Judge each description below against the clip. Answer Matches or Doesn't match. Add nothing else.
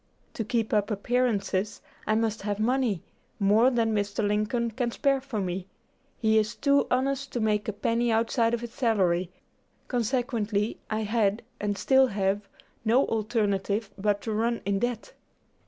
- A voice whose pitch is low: Doesn't match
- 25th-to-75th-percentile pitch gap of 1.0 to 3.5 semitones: Matches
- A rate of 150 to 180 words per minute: Matches